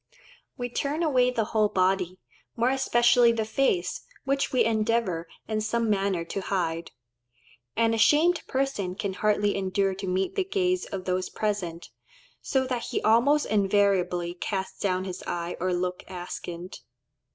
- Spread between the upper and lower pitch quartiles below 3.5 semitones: No, average, 4.7 semitones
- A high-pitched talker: Yes, high, 205 Hz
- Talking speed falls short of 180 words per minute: Yes, average, 150 wpm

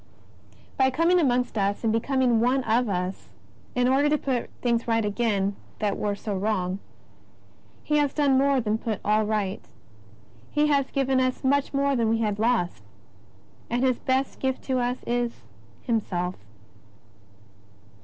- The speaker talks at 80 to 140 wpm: No, average, 155 wpm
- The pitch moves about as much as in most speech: Yes, average, 4.0 semitones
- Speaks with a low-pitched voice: No, high, 240 Hz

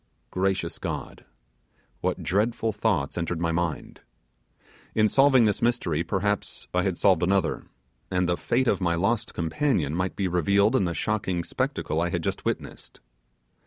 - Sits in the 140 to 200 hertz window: No, very low, 95 Hz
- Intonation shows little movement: No, average, 3.8 semitones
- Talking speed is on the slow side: No, average, 155 wpm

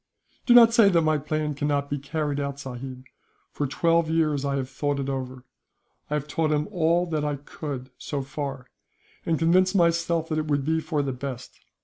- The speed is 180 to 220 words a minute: Yes, average, 195 wpm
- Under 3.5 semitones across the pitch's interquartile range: Yes, average, 2.8 semitones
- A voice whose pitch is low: No, medium, 150 Hz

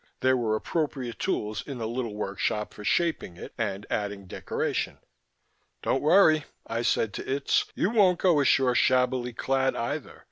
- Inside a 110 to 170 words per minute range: Yes, average, 155 wpm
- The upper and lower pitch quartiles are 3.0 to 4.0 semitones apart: No, average, 4.9 semitones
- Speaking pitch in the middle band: No, low, 125 Hz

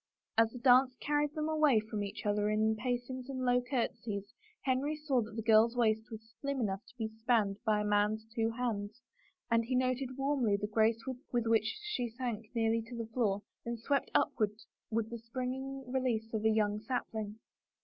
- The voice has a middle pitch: No, high, 230 Hz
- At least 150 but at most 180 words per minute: No, average, 190 wpm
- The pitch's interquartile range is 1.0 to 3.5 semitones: Yes, average, 2.8 semitones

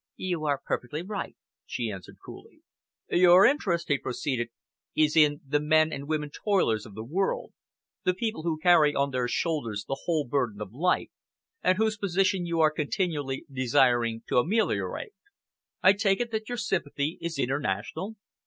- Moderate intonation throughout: No, wide, 5.7 semitones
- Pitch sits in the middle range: Yes, medium, 155 Hz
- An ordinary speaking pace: Yes, average, 160 wpm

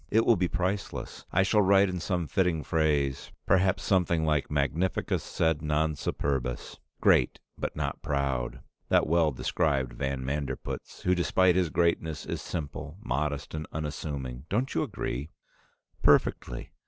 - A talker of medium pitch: No, very low, 80 Hz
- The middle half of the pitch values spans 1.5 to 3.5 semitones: No, average, 4.3 semitones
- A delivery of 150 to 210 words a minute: No, average, 140 wpm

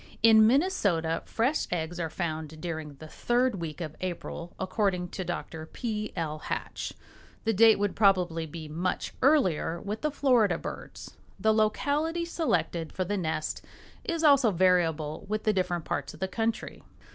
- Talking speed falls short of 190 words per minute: Yes, average, 155 wpm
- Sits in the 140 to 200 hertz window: Yes, medium, 185 Hz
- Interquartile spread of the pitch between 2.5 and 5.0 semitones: No, wide, 5.5 semitones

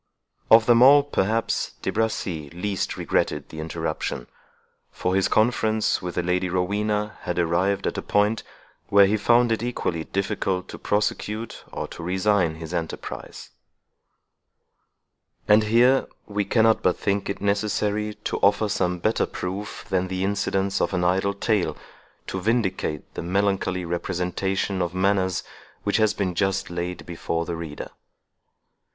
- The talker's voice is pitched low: Yes, very low, 95 Hz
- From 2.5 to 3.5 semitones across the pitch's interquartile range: Yes, average, 2.9 semitones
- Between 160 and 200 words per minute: No, average, 145 wpm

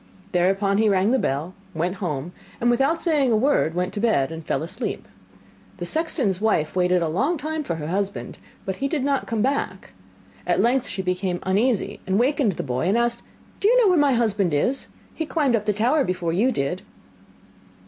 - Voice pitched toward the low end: No, high, 205 Hz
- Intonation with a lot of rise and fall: Yes, wide, 6.7 semitones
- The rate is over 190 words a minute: Yes, average, 200 wpm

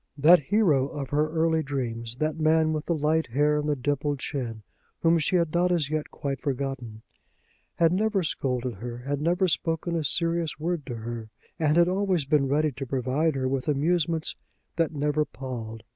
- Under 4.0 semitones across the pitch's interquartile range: Yes, average, 3.6 semitones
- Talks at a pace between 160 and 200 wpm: Yes, average, 185 wpm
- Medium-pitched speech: Yes, medium, 150 Hz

